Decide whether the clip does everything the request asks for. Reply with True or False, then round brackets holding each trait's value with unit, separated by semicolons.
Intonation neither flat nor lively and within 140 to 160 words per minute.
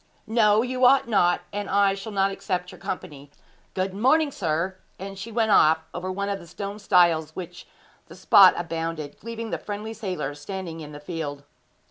False (3.9 semitones; 185 wpm)